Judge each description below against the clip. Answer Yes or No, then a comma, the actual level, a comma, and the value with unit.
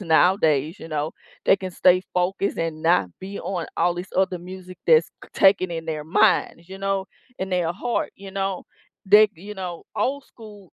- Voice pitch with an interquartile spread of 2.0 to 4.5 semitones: Yes, average, 2.7 semitones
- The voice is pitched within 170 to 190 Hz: Yes, medium, 185 Hz